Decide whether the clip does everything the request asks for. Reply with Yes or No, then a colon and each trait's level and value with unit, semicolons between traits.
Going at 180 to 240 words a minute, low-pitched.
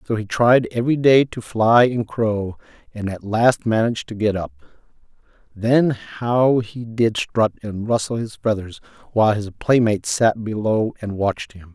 No: average, 170 wpm; low, 110 Hz